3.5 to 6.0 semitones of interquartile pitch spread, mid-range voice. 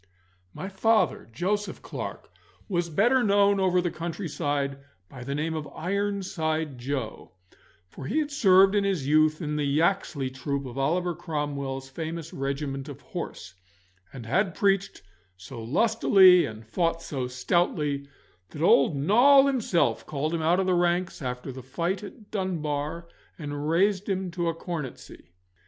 Yes: average, 5.3 semitones; medium, 165 Hz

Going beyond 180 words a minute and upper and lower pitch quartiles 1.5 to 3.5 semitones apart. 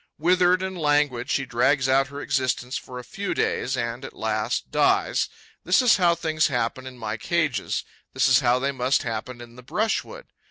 No: average, 190 wpm; average, 4.8 semitones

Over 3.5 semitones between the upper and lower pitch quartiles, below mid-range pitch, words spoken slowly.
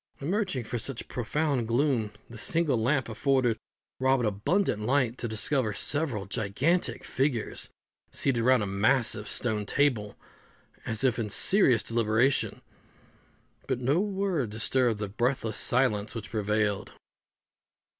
Yes: average, 4.0 semitones; low, 120 Hz; slow, 125 wpm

